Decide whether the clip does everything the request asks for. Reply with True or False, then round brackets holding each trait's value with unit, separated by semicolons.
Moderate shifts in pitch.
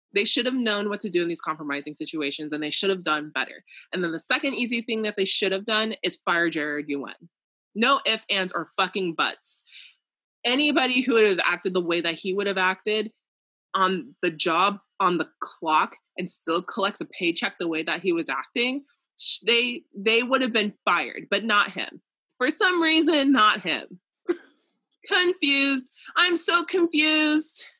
False (7.7 semitones)